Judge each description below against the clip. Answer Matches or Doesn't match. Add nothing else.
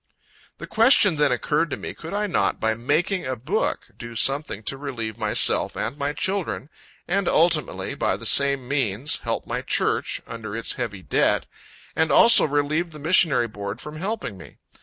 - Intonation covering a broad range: Matches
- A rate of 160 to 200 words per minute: Matches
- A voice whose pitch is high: Doesn't match